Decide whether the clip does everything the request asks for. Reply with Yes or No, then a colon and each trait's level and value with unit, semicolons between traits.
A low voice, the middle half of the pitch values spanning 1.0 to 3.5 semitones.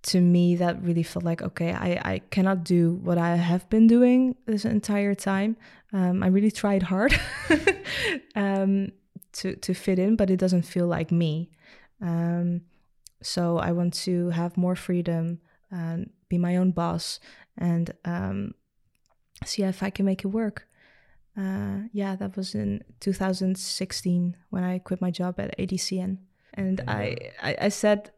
No: medium, 185 Hz; narrow, 2.4 semitones